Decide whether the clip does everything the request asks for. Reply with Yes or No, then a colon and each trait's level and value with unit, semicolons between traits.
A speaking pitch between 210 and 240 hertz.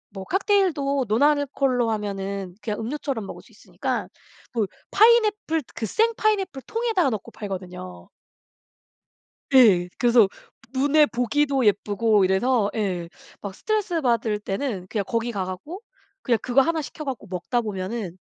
Yes: high, 235 Hz